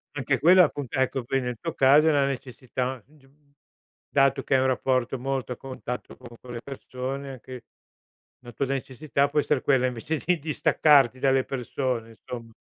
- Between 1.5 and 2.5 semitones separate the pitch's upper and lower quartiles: Yes, narrow, 1.9 semitones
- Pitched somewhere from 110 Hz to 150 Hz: Yes, low, 135 Hz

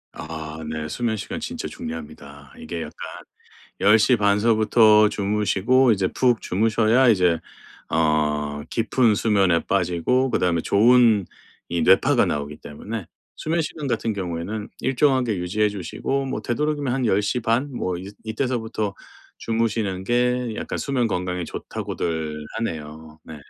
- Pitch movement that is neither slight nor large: No, wide, 5.9 semitones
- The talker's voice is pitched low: Yes, low, 105 Hz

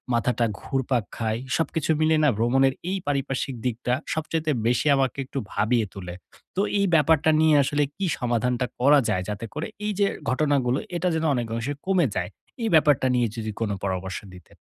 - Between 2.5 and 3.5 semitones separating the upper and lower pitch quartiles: No, average, 4.7 semitones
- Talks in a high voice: No, low, 130 Hz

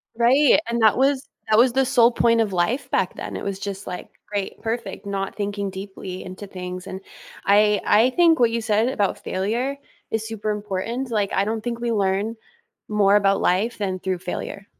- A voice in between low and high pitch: No, high, 210 Hz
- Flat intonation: No, average, 3.2 semitones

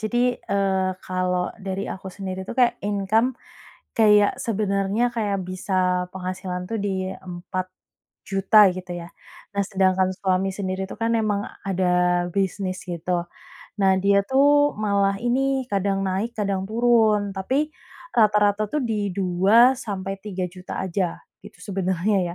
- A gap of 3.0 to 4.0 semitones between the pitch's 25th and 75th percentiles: No, narrow, 2.4 semitones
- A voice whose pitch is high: Yes, high, 195 Hz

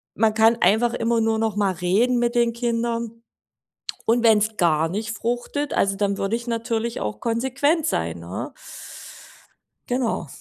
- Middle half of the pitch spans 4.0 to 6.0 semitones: No, average, 2.8 semitones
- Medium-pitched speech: No, high, 225 Hz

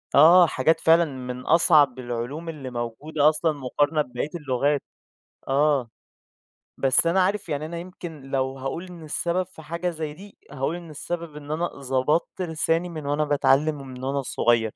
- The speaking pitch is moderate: Yes, medium, 150 Hz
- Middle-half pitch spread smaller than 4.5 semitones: Yes, average, 3.8 semitones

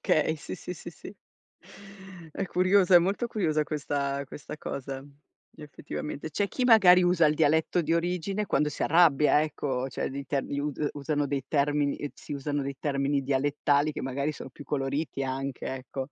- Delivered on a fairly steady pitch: No, average, 3.0 semitones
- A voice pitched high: No, medium, 145 Hz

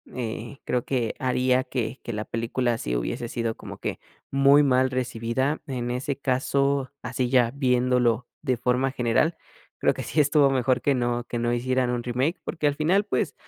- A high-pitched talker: No, low, 125 Hz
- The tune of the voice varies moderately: No, narrow, 2.2 semitones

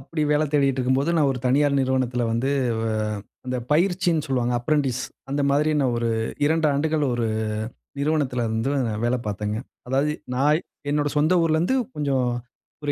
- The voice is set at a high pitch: No, medium, 140 Hz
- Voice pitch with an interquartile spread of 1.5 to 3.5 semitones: Yes, average, 3.1 semitones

